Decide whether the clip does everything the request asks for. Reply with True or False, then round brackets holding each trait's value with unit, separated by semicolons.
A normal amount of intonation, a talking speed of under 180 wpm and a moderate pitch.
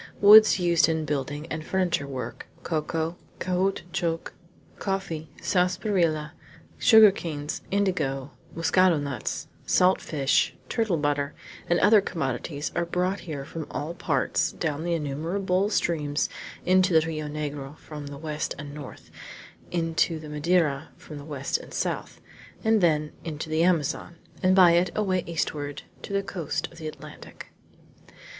True (3.5 semitones; 140 wpm; 165 Hz)